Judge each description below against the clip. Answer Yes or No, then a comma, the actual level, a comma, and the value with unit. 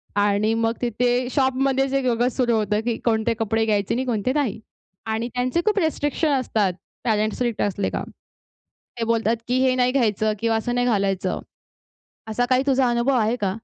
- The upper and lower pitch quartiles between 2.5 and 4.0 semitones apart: Yes, average, 2.9 semitones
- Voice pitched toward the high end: Yes, high, 235 Hz